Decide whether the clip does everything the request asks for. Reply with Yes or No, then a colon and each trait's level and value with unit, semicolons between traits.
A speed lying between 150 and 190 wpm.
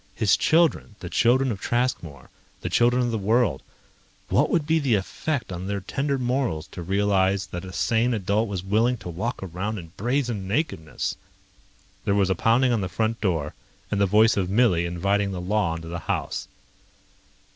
Yes: average, 180 wpm